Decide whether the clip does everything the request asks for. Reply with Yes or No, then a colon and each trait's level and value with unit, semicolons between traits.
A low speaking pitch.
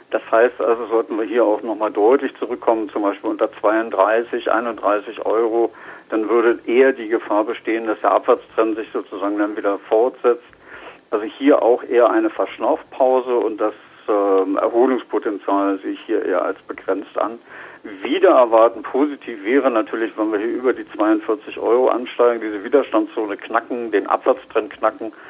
Yes: low, 115 Hz